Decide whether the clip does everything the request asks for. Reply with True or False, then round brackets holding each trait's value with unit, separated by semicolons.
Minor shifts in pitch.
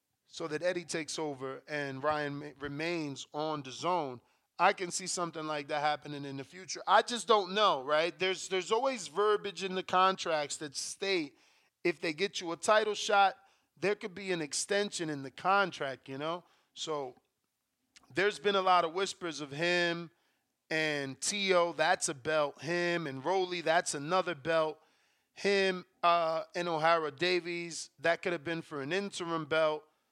False (3.7 semitones)